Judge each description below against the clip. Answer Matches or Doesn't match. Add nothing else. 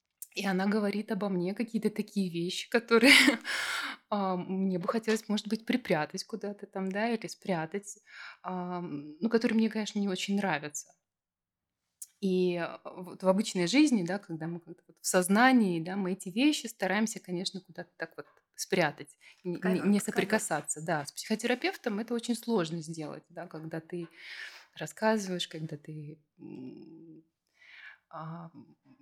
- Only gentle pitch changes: Doesn't match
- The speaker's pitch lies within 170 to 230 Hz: Matches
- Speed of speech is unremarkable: Matches